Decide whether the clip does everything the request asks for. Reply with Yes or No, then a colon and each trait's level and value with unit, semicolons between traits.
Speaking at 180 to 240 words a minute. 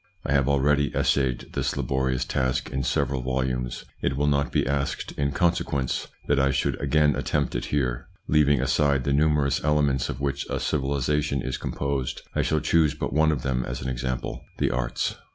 Yes: average, 185 wpm